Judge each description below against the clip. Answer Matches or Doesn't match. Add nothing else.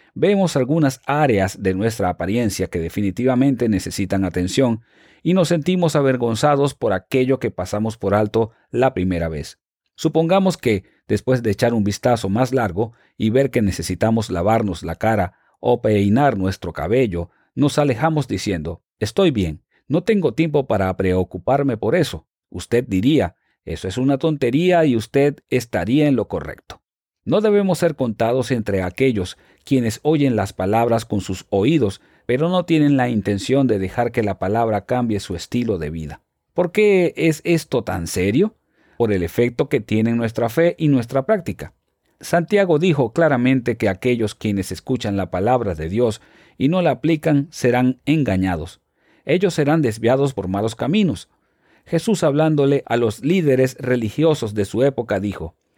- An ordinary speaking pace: Matches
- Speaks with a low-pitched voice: Matches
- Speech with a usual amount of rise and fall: Doesn't match